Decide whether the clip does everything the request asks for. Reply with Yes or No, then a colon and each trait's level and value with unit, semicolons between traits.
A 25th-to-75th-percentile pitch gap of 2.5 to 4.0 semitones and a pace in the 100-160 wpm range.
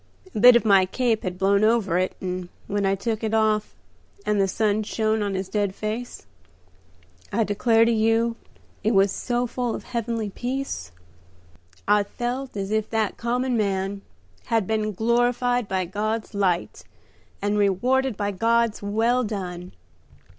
Yes: average, 2.9 semitones; average, 155 wpm